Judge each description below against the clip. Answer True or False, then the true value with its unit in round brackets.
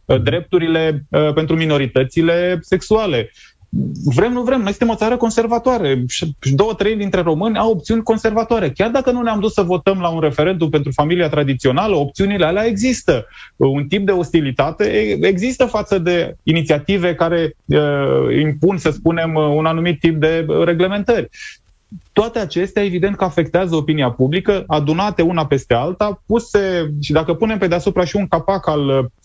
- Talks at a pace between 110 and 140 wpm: False (150 wpm)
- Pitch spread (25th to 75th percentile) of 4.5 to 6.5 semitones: True (5.1 semitones)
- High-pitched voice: False (175 Hz)